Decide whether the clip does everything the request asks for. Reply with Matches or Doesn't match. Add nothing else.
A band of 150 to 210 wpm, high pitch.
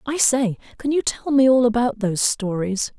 Matches